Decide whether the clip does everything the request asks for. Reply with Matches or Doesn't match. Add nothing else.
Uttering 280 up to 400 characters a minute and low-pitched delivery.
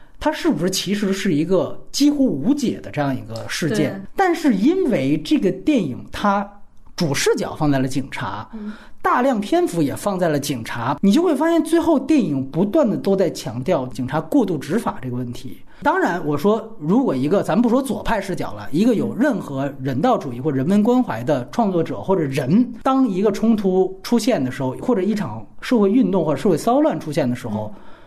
Doesn't match